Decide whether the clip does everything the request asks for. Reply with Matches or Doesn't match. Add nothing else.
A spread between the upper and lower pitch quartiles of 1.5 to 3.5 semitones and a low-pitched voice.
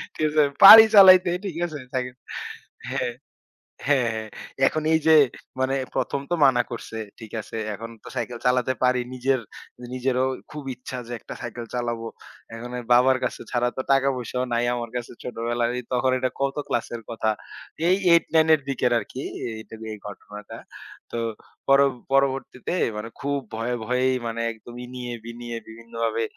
Matches